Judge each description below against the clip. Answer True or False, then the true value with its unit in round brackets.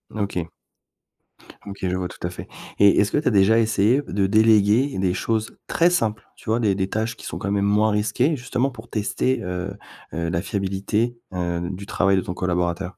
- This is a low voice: True (100 Hz)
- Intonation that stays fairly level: False (3.2 semitones)